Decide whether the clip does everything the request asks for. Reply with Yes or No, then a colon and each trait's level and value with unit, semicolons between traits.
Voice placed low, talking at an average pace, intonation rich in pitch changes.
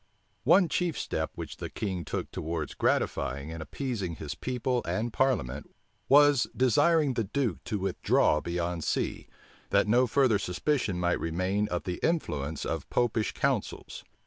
Yes: low, 105 Hz; average, 145 wpm; wide, 7.3 semitones